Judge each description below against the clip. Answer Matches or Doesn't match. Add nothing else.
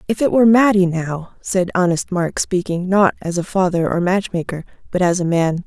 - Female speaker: Matches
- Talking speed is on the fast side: Matches